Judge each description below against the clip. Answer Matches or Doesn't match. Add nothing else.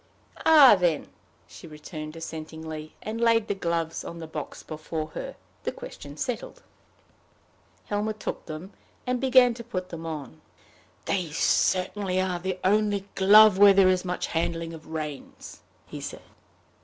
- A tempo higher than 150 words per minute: Doesn't match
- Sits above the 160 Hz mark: Matches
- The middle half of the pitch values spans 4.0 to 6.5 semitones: Matches